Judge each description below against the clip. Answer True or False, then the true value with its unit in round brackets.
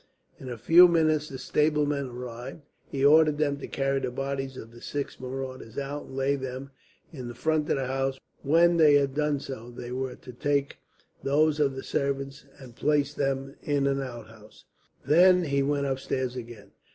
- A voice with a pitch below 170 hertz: True (135 Hz)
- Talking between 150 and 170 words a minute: False (180 wpm)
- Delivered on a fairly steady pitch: True (2.1 semitones)